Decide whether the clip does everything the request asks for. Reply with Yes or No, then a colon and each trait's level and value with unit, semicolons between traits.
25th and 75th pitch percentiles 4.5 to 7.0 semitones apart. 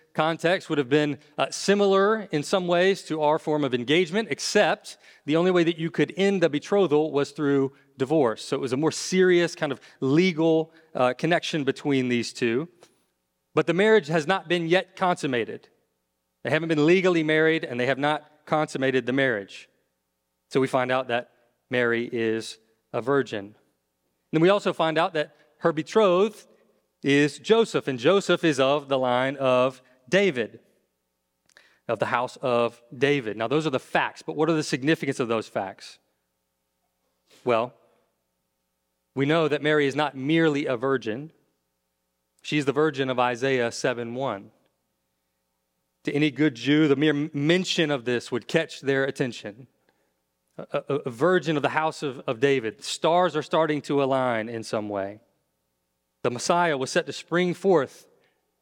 Yes: wide, 5.5 semitones